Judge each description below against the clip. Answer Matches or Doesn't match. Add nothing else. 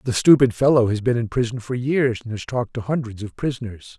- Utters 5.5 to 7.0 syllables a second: Matches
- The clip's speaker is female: Doesn't match